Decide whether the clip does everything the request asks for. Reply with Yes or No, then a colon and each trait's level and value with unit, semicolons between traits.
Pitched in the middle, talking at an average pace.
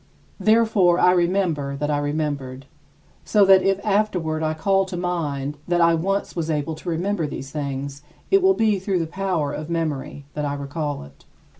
Yes: medium, 165 Hz; average, 180 wpm